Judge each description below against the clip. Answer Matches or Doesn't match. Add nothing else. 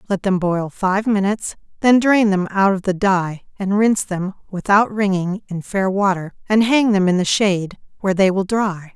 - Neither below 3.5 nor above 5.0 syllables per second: Matches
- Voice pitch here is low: Doesn't match